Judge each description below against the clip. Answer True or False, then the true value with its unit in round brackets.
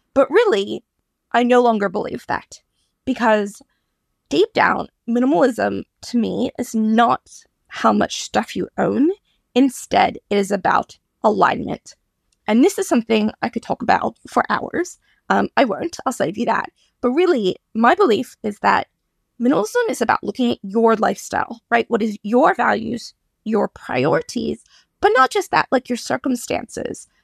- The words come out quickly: False (150 wpm)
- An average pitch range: True (4.2 semitones)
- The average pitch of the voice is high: True (245 Hz)